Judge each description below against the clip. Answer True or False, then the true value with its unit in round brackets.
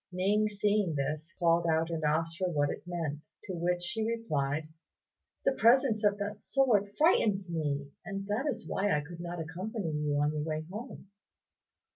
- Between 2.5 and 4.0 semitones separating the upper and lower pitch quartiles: False (4.9 semitones)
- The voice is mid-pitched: True (175 Hz)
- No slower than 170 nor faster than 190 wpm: True (175 wpm)